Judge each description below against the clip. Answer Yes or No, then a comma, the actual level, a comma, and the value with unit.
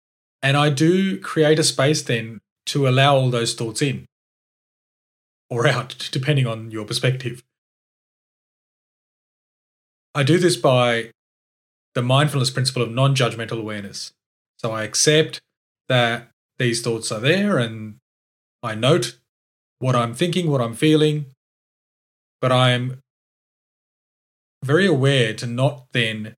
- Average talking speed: No, slow, 125 wpm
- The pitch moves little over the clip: No, average, 3.7 semitones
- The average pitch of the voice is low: Yes, low, 125 Hz